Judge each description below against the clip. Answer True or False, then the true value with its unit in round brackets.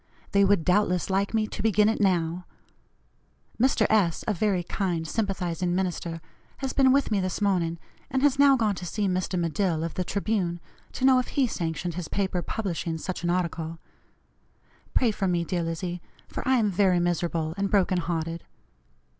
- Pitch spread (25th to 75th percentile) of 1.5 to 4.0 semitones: True (3.6 semitones)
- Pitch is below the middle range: False (185 Hz)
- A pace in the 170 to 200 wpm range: True (180 wpm)